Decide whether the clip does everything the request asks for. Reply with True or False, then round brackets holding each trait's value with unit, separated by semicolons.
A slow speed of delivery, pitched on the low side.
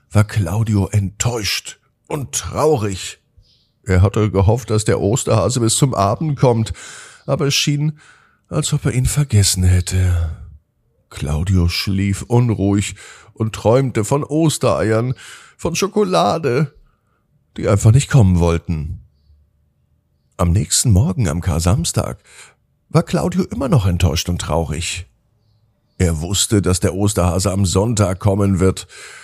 True (120 wpm; 105 Hz)